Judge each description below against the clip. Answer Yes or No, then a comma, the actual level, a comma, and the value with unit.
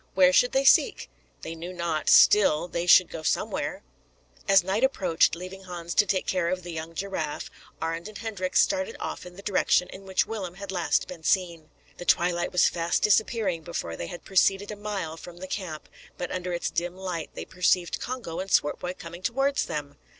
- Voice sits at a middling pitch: Yes, medium, 180 Hz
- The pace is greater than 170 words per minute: Yes, average, 195 wpm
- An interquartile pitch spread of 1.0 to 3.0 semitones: Yes, narrow, 2.6 semitones